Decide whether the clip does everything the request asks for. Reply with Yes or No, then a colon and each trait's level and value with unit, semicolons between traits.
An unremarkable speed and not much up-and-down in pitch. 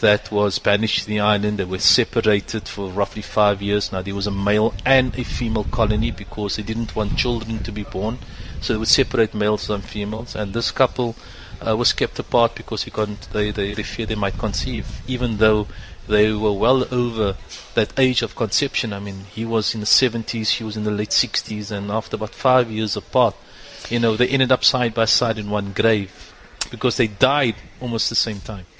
No: fast, 210 wpm; narrow, 2.2 semitones